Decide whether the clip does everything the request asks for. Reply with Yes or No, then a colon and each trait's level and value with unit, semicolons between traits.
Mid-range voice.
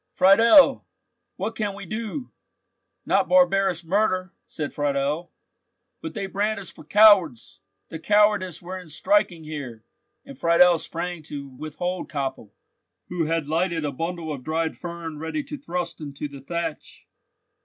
Yes: medium, 170 Hz